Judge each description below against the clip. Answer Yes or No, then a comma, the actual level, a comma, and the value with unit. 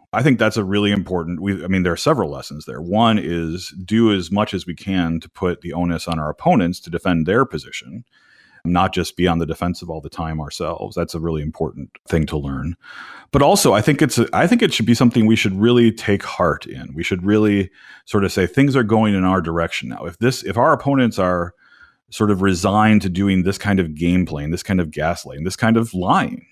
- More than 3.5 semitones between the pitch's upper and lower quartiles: Yes, average, 4.0 semitones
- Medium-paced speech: No, fast, 240 wpm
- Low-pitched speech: Yes, very low, 95 Hz